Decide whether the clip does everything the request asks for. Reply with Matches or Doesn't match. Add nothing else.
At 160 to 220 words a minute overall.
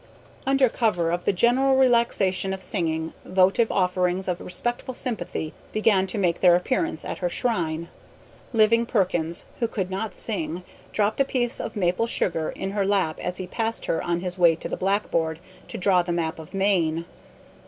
Matches